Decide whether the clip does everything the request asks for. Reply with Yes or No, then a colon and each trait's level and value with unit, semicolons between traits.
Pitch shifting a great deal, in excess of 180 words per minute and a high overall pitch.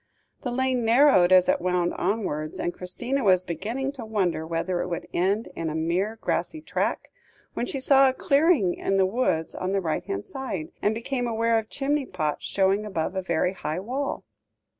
Yes: wide, 6.1 semitones; average, 190 wpm; high, 195 Hz